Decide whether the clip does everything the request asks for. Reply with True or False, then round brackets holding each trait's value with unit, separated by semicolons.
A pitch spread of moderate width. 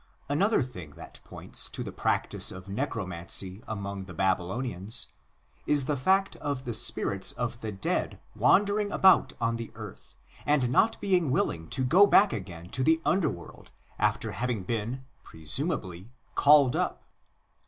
False (7.5 semitones)